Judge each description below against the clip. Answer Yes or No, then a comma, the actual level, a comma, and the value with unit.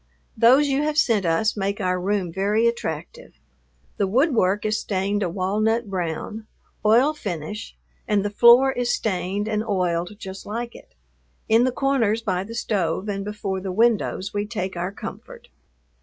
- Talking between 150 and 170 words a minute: Yes, average, 160 wpm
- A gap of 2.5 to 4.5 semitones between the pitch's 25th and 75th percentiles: Yes, average, 3.5 semitones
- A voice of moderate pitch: No, high, 210 Hz